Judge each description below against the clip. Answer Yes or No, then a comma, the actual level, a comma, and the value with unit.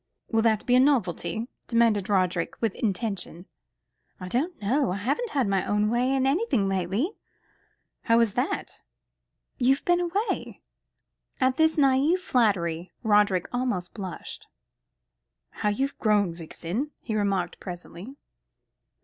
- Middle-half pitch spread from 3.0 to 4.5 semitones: No, wide, 5.5 semitones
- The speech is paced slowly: Yes, slow, 130 wpm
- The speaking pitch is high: Yes, high, 225 Hz